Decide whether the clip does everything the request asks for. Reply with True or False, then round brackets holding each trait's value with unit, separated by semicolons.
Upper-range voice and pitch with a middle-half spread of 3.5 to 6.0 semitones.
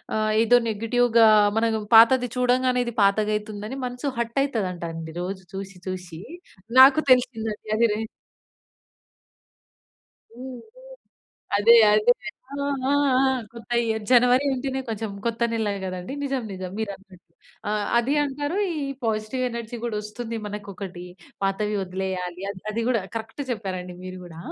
True (220 Hz; 3.8 semitones)